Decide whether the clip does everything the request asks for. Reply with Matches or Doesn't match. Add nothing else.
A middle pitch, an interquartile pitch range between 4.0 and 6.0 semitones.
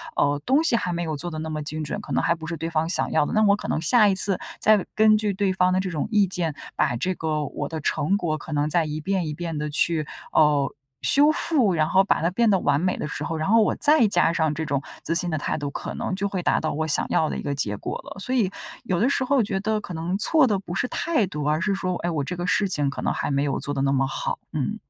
Matches